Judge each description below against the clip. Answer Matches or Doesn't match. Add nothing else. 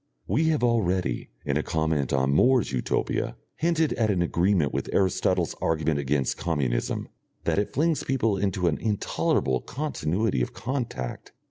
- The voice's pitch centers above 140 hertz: Doesn't match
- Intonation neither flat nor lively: Doesn't match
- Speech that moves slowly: Doesn't match